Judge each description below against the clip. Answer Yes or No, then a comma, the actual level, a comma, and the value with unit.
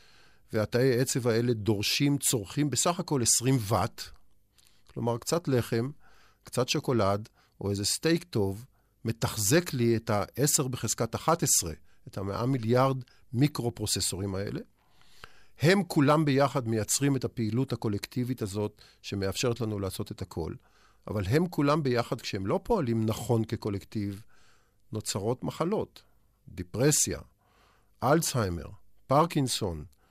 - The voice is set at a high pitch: No, low, 115 Hz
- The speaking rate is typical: Yes, average, 115 wpm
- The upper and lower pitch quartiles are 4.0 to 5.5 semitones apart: Yes, average, 4.8 semitones